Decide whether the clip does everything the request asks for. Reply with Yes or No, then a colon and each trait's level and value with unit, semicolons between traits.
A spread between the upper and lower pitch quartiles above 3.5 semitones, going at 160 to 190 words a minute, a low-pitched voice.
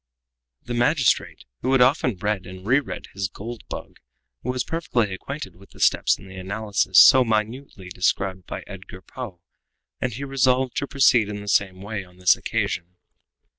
Yes: average, 5.2 semitones; average, 170 wpm; low, 105 Hz